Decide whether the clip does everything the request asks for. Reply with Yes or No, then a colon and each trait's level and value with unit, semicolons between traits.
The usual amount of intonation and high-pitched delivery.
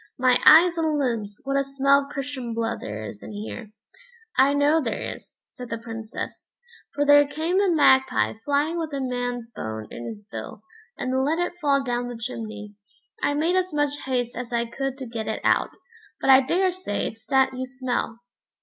Yes: average, 3.9 semitones; very high, 260 Hz